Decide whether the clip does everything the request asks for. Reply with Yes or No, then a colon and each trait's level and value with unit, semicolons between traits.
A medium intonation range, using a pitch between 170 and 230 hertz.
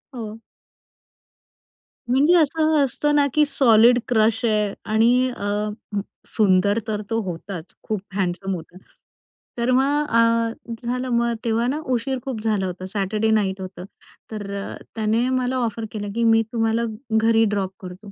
Yes: average, 3.5 semitones; high, 225 Hz